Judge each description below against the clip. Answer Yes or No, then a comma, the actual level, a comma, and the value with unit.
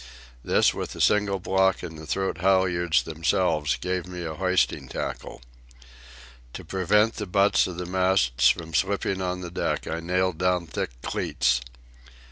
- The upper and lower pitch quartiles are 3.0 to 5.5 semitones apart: No, narrow, 2.5 semitones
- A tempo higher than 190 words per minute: No, average, 155 wpm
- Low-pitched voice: Yes, very low, 90 Hz